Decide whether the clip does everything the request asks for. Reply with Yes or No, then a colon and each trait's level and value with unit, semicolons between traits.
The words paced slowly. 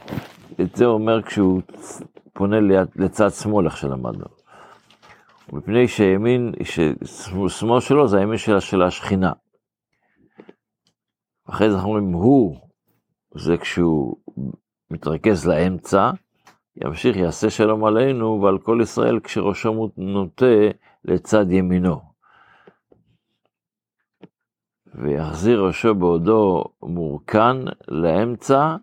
Yes: slow, 90 wpm